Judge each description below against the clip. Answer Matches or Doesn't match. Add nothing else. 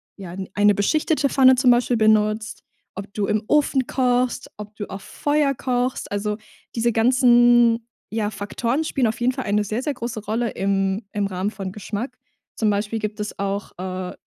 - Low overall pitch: Doesn't match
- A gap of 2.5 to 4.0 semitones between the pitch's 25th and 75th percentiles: Matches